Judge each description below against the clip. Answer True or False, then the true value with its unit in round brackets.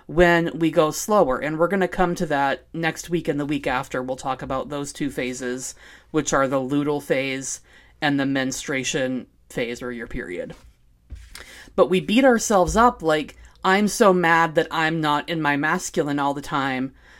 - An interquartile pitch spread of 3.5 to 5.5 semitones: True (4.3 semitones)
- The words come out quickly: False (185 wpm)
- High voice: False (145 Hz)